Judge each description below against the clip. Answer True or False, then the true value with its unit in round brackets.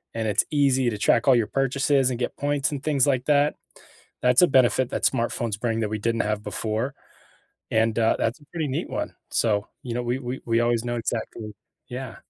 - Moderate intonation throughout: True (3.1 semitones)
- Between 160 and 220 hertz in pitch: False (120 Hz)